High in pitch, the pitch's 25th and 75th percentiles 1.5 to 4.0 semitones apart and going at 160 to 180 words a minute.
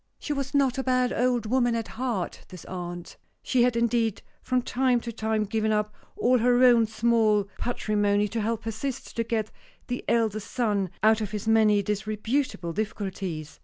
Yes: high, 225 Hz; average, 2.7 semitones; average, 175 wpm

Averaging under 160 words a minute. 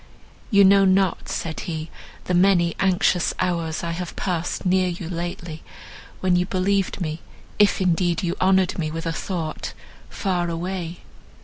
Yes: average, 150 wpm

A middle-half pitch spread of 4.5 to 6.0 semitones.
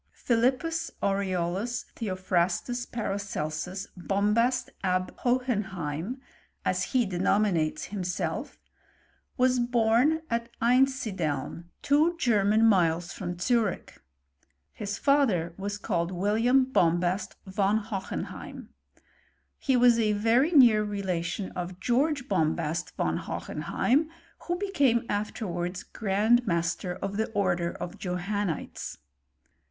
Yes: average, 5.2 semitones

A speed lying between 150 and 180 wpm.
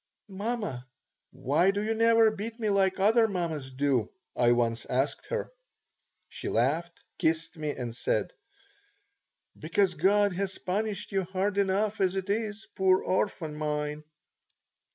No: slow, 135 wpm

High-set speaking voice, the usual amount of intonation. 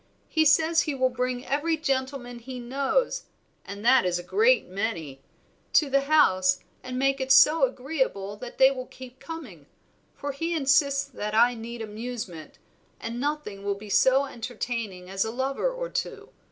Yes: very high, 255 Hz; average, 4.3 semitones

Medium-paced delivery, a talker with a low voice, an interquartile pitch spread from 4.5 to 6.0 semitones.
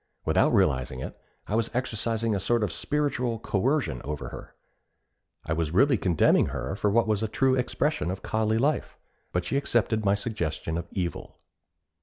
Yes: average, 170 wpm; low, 110 Hz; wide, 5.5 semitones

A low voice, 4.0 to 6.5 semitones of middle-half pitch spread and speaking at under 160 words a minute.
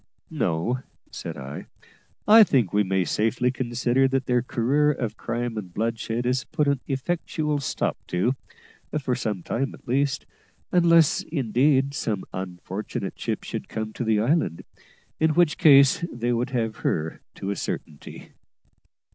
Yes: low, 125 Hz; average, 4.4 semitones; average, 145 wpm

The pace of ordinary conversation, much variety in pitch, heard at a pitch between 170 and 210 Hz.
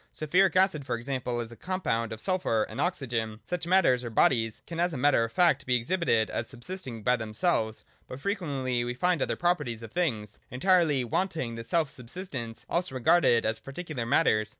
No: average, 185 wpm; wide, 7.0 semitones; low, 130 Hz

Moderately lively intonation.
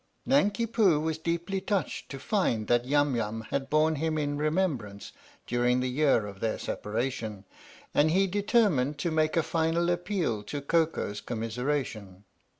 No: wide, 5.9 semitones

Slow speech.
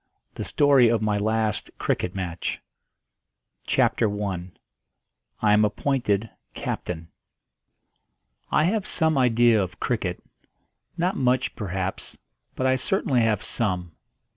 Yes: slow, 115 wpm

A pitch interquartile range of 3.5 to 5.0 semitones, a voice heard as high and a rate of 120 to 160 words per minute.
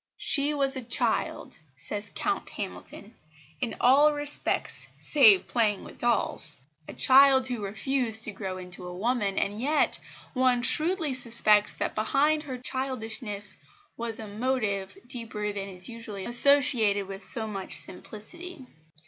Yes: average, 4.5 semitones; high, 235 Hz; average, 140 wpm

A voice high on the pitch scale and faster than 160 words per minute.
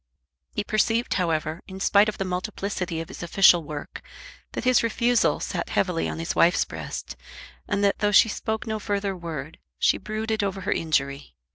Yes: high, 195 Hz; average, 175 wpm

